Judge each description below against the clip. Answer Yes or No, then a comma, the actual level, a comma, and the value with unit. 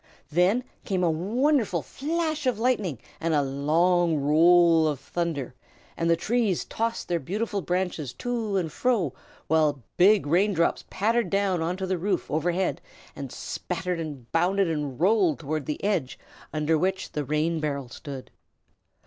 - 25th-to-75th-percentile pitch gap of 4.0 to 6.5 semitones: Yes, average, 4.5 semitones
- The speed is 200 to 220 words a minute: No, average, 155 wpm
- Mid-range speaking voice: Yes, medium, 175 Hz